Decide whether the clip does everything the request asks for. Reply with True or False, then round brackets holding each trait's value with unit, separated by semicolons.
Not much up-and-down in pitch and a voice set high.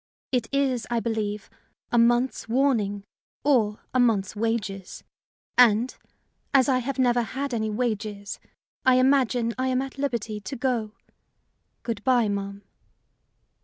False (3.4 semitones; 235 Hz)